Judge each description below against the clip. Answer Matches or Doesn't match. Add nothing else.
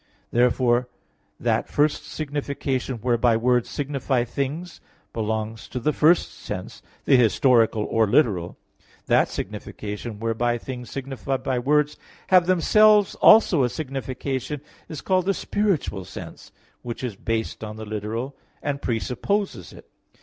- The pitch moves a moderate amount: Matches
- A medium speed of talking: Doesn't match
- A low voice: Matches